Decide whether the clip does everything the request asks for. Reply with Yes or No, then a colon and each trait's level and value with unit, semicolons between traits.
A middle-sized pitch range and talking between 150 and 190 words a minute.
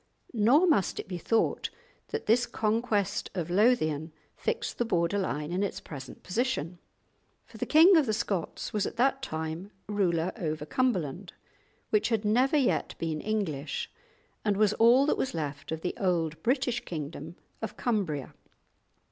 No: wide, 6.8 semitones; average, 155 wpm